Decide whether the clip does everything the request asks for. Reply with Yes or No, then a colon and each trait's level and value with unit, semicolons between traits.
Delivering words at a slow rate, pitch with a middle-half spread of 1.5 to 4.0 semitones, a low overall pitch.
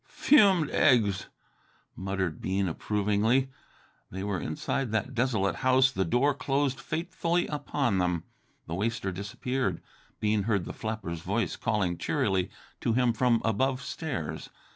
No: slow, 130 wpm; wide, 5.5 semitones; low, 115 Hz